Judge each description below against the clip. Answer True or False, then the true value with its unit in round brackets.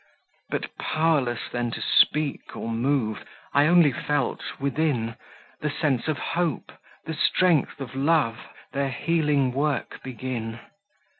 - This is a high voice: False (140 Hz)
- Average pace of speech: False (125 wpm)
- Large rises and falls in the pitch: False (4.0 semitones)